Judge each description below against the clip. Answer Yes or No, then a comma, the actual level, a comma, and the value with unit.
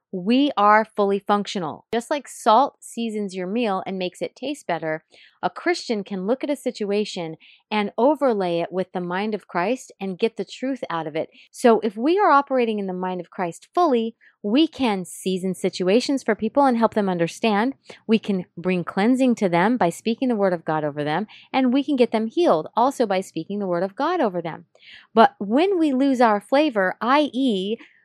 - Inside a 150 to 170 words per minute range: No, average, 200 wpm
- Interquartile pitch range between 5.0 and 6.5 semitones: Yes, average, 5.3 semitones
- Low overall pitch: No, high, 215 Hz